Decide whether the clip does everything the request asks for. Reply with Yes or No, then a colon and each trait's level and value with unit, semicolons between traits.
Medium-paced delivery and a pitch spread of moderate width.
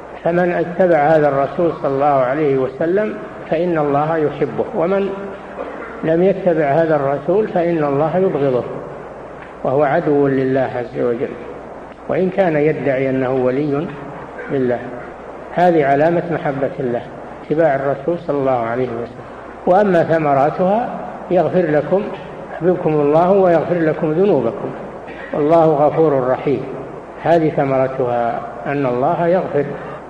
Yes: average, 115 wpm; average, 3.9 semitones